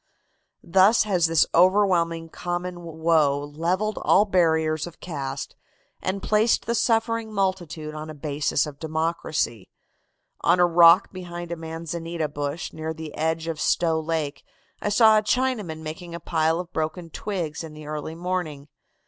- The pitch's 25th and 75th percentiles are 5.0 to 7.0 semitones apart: No, average, 2.8 semitones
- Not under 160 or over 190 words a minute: No, average, 150 wpm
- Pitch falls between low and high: Yes, medium, 165 Hz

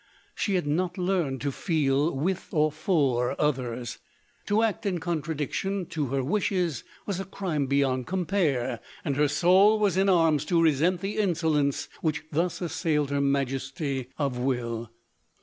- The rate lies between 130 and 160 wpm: Yes, average, 150 wpm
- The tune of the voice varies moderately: Yes, average, 4.8 semitones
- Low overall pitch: No, medium, 155 Hz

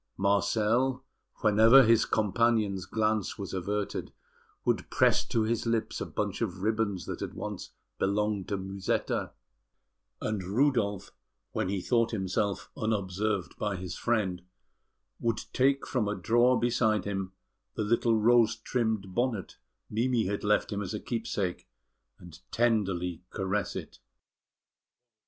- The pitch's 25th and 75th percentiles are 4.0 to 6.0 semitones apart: No, average, 3.0 semitones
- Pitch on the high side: No, low, 105 Hz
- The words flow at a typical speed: No, slow, 130 wpm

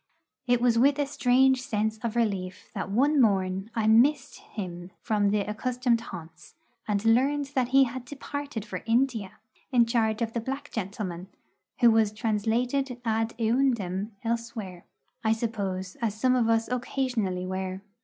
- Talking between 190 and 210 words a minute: No, average, 155 wpm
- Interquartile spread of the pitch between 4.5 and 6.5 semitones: No, average, 3.5 semitones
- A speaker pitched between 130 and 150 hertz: No, high, 225 Hz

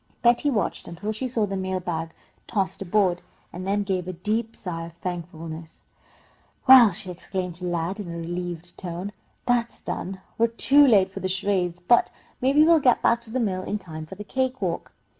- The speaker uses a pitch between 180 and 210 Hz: Yes, high, 190 Hz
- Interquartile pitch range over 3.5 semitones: Yes, average, 4.4 semitones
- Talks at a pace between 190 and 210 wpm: Yes, average, 195 wpm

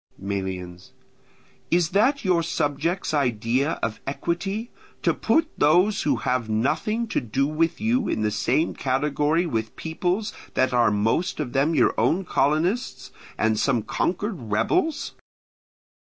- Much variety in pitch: Yes, wide, 7.5 semitones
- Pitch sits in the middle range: Yes, medium, 145 Hz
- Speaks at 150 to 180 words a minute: No, slow, 135 wpm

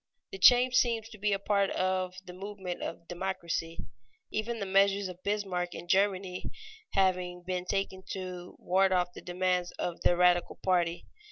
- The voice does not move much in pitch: Yes, narrow, 1.9 semitones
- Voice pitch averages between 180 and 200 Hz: Yes, medium, 185 Hz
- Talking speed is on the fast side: No, average, 165 wpm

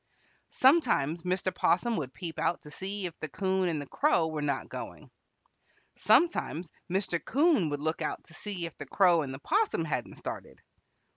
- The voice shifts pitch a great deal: No, average, 4.5 semitones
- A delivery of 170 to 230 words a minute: Yes, average, 175 wpm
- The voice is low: No, medium, 175 Hz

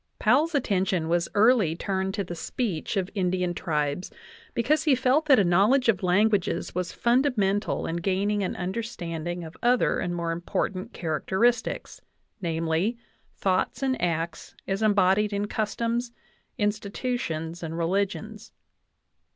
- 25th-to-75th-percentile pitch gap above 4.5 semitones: Yes, average, 4.9 semitones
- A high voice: Yes, high, 195 Hz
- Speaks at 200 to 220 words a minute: No, slow, 135 wpm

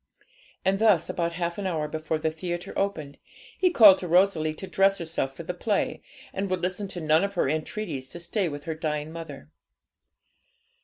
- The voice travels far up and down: No, average, 3.6 semitones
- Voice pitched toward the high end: No, medium, 170 Hz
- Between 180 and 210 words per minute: Yes, average, 190 wpm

